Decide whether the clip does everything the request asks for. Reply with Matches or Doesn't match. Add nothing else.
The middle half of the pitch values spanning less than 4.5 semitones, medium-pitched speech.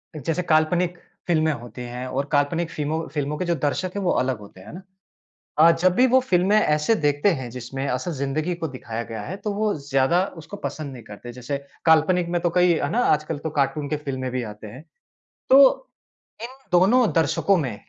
Doesn't match